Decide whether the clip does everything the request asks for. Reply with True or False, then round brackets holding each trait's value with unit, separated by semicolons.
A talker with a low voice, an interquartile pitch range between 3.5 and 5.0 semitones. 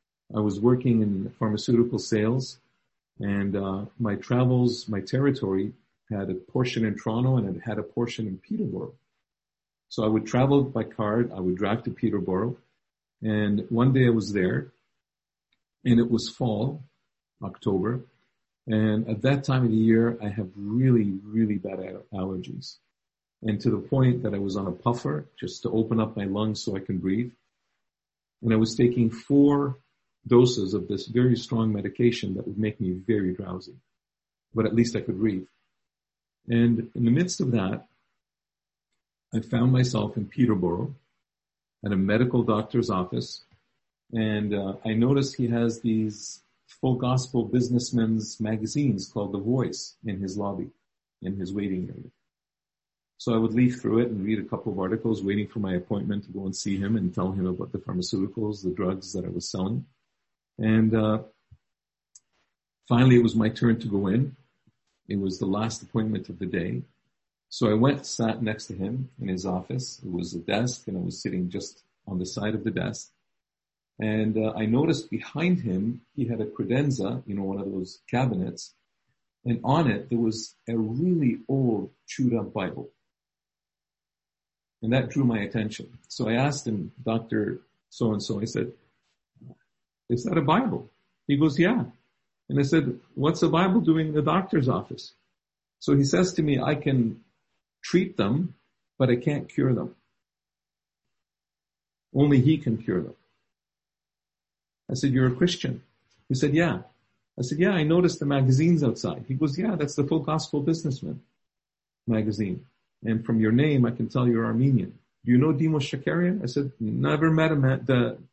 True (115 Hz; 4.1 semitones)